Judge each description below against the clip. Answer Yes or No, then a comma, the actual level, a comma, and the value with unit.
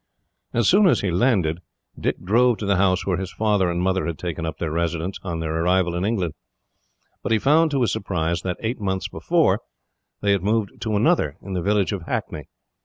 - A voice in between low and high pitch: No, very low, 95 Hz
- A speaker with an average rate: No, fast, 210 wpm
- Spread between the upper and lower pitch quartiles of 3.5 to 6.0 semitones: Yes, average, 3.9 semitones